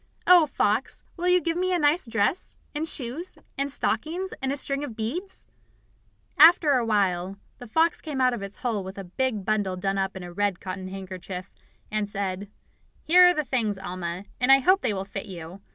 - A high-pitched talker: Yes, high, 220 Hz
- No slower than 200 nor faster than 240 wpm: Yes, fast, 205 wpm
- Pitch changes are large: Yes, wide, 7.6 semitones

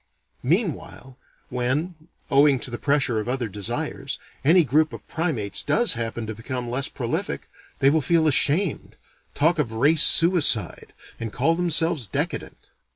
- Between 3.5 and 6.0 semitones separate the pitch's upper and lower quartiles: Yes, average, 4.9 semitones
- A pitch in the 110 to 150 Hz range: Yes, medium, 140 Hz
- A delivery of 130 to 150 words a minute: Yes, average, 145 wpm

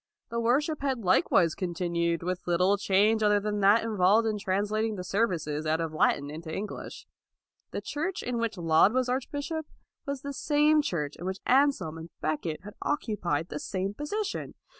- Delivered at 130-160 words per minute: No, average, 175 wpm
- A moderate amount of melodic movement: No, wide, 6.5 semitones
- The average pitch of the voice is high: Yes, high, 205 Hz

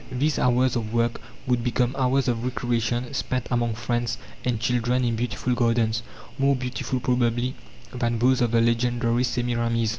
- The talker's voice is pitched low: Yes, low, 120 Hz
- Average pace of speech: Yes, average, 155 wpm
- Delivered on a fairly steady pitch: Yes, narrow, 1.3 semitones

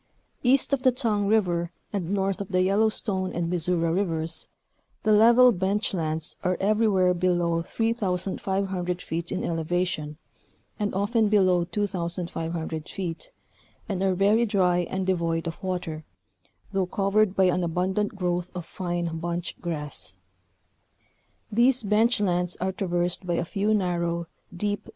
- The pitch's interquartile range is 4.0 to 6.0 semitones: No, average, 3.0 semitones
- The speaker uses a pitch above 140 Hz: Yes, medium, 185 Hz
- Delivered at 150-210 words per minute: No, average, 140 wpm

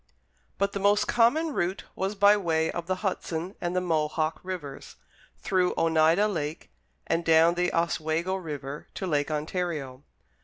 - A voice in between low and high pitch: Yes, medium, 170 Hz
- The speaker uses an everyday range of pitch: Yes, average, 3.2 semitones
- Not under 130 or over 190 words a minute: Yes, average, 150 wpm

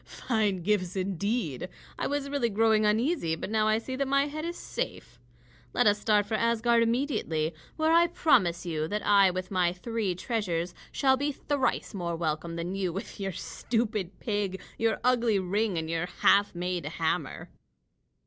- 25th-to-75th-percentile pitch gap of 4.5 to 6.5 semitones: Yes, average, 4.9 semitones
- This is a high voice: Yes, high, 205 Hz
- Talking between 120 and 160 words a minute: No, average, 170 wpm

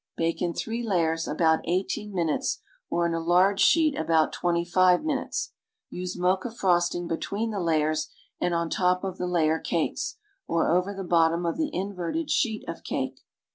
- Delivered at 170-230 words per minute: Yes, average, 175 wpm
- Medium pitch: Yes, medium, 175 Hz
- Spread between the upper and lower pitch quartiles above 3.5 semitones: No, average, 2.8 semitones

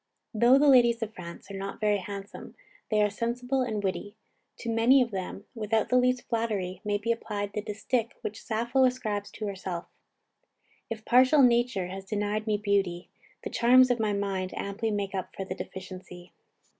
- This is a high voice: Yes, high, 210 Hz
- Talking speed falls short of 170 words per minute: No, average, 180 wpm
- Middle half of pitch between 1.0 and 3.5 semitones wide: Yes, average, 3.2 semitones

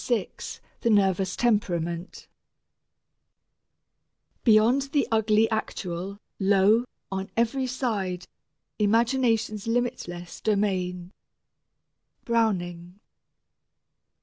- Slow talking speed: Yes, slow, 70 wpm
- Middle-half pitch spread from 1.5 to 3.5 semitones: No, average, 3.9 semitones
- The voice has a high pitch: Yes, high, 210 Hz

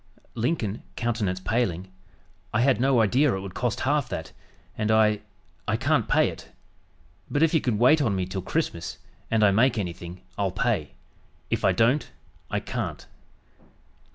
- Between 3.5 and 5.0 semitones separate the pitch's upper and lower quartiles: Yes, average, 4.6 semitones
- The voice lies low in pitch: Yes, low, 110 Hz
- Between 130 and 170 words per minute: Yes, average, 160 wpm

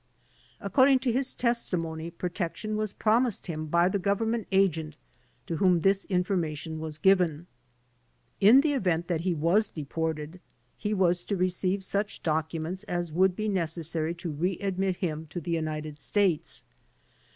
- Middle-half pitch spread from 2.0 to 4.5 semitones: Yes, average, 3.7 semitones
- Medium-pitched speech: Yes, medium, 180 Hz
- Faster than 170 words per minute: No, average, 150 wpm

